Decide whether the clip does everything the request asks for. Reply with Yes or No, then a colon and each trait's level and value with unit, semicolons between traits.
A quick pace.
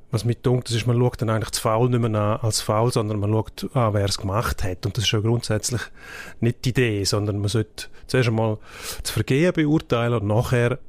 Yes: fast, 225 wpm